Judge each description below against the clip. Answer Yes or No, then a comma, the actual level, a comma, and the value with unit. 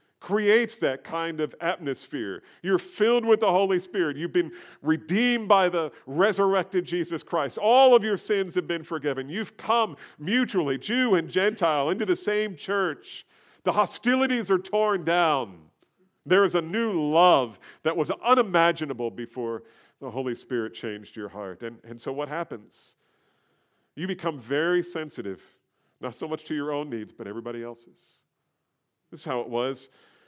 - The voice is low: No, medium, 170 Hz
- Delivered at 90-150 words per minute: No, average, 160 wpm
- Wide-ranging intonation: Yes, wide, 6.2 semitones